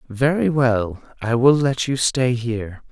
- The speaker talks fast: No, average, 165 wpm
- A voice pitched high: No, low, 125 Hz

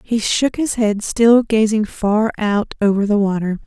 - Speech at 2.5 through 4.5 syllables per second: Yes, 4.1 syllables/s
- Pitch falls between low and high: No, high, 215 Hz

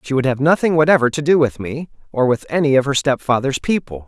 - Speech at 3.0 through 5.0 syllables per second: No, 6.1 syllables/s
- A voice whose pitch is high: No, medium, 140 Hz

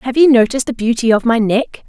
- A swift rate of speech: Yes, fast, 255 wpm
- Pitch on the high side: Yes, high, 240 Hz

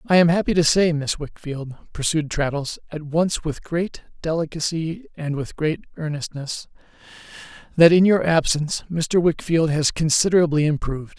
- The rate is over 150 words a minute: No, average, 145 wpm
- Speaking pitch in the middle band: Yes, medium, 160 Hz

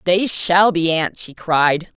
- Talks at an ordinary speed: Yes, average, 180 wpm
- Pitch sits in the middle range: Yes, medium, 175 Hz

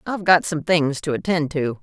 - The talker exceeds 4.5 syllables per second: Yes, 5.3 syllables/s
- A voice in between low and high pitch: Yes, medium, 160 Hz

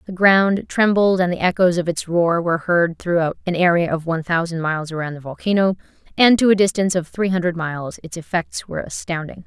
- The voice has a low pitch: No, medium, 175 Hz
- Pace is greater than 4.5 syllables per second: Yes, 5.8 syllables/s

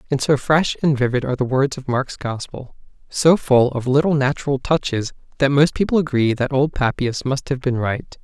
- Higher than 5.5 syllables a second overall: No, 5.2 syllables/s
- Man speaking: Yes, male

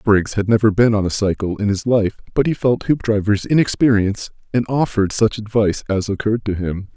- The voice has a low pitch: Yes, low, 110 Hz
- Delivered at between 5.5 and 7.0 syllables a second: Yes, 5.8 syllables/s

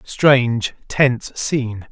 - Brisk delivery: No, slow, 95 wpm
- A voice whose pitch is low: Yes, low, 125 Hz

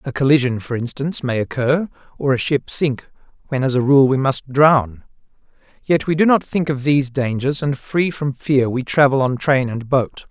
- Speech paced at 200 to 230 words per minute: Yes, fast, 205 wpm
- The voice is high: No, low, 135 Hz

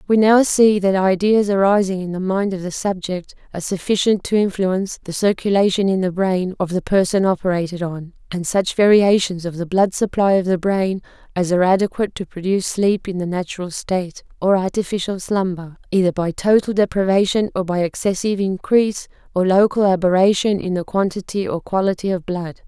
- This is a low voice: No, high, 190 Hz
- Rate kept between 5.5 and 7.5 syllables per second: Yes, 5.6 syllables/s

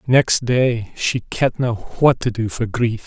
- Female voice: No, male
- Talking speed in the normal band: Yes, average, 175 wpm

